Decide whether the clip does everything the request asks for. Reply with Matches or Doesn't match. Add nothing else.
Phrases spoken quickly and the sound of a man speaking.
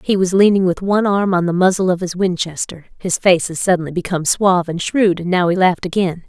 Doesn't match